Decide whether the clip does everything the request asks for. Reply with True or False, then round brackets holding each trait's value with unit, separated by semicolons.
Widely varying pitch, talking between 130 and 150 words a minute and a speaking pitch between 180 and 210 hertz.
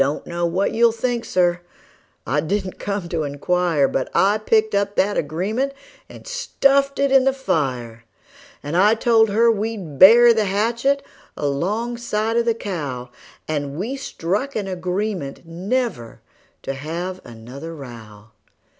True (7.2 semitones; 145 wpm; 190 Hz)